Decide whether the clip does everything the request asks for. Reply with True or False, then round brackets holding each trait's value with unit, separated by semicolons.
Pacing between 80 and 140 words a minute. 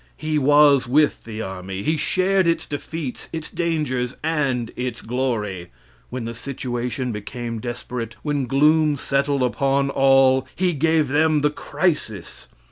True (135 wpm)